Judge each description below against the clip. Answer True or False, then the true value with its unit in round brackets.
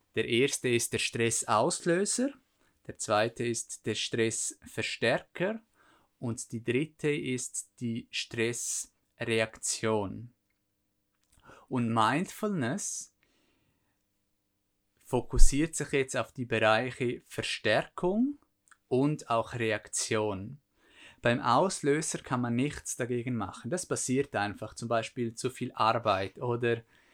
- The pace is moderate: False (95 wpm)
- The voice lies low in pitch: True (120 Hz)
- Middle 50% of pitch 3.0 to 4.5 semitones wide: True (3.9 semitones)